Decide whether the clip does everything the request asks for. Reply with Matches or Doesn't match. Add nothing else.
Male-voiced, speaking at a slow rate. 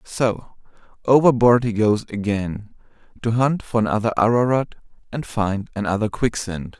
Matches